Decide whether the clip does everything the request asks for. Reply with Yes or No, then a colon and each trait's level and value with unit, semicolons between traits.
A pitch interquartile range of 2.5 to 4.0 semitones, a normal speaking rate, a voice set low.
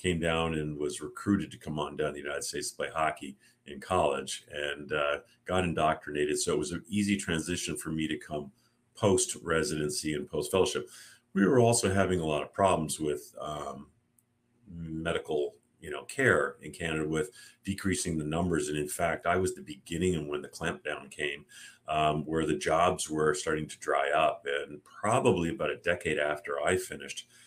Yes: average, 3.6 semitones; average, 190 wpm; very low, 80 Hz